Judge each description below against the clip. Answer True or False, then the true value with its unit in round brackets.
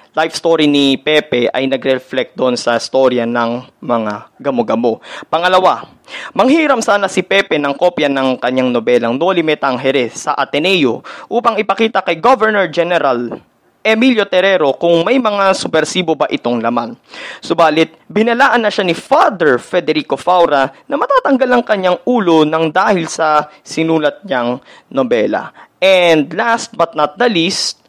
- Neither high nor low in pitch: True (165 Hz)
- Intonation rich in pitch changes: True (6.5 semitones)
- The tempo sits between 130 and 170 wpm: True (140 wpm)